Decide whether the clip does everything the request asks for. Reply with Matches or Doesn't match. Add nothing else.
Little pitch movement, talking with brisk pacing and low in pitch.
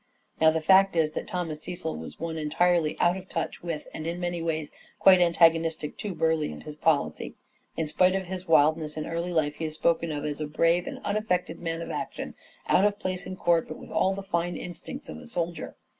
Doesn't match